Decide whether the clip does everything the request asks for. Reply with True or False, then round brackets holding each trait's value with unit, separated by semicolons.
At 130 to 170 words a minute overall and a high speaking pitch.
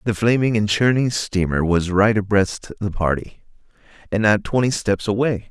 False (165 wpm; 105 Hz)